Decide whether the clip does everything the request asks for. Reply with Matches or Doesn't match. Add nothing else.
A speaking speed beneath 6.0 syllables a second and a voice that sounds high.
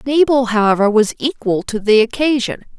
Matches